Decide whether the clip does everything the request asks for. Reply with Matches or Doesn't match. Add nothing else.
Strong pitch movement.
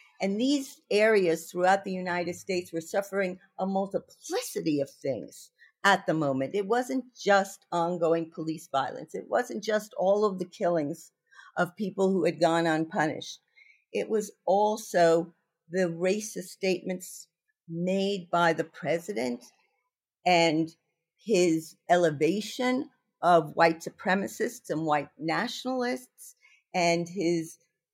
Doesn't match